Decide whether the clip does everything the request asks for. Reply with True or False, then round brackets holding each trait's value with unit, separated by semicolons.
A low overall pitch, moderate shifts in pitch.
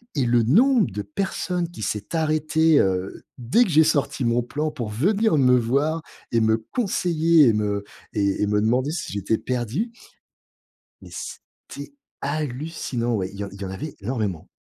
False (125 Hz; 6.8 semitones)